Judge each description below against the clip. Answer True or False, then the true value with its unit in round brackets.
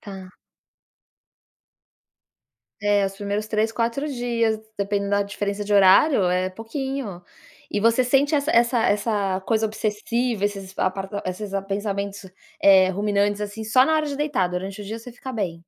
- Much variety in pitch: False (2.9 semitones)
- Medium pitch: False (205 Hz)